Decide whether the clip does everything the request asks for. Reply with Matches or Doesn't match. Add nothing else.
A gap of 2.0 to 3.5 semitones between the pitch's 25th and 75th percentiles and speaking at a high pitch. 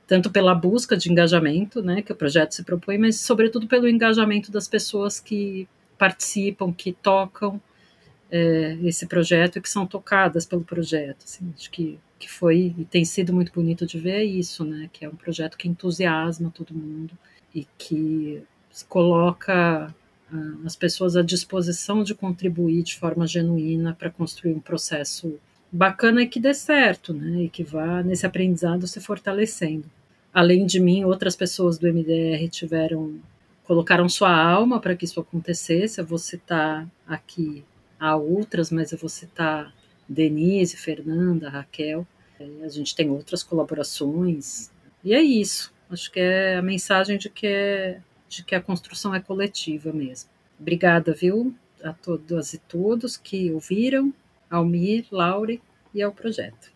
Doesn't match